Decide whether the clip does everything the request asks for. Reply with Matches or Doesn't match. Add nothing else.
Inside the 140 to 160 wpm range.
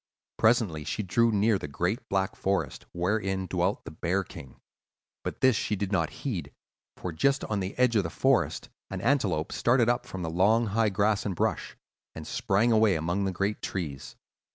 Doesn't match